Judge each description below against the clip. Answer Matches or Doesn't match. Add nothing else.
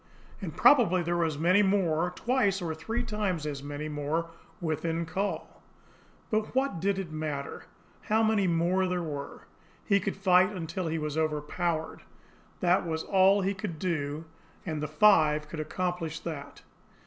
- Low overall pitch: Doesn't match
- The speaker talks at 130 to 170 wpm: Matches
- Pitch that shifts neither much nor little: Matches